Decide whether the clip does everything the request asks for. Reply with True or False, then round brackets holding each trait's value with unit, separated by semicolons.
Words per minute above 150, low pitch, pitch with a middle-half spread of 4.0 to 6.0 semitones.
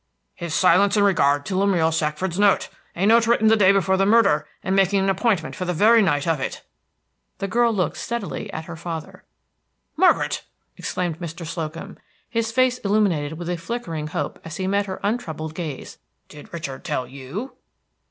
False (180 wpm; 185 Hz; 4.3 semitones)